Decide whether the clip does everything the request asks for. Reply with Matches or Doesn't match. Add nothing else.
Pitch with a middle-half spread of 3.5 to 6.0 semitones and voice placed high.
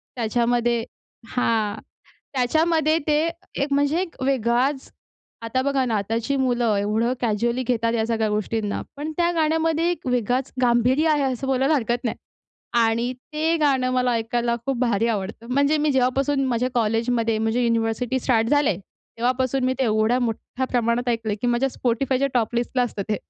Doesn't match